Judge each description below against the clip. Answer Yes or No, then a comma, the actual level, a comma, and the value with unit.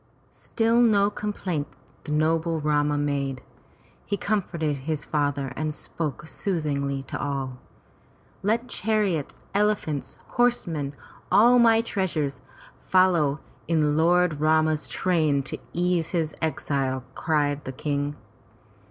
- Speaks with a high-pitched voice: No, medium, 155 Hz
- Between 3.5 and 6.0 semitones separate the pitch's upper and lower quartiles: Yes, average, 4.5 semitones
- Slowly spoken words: Yes, slow, 115 wpm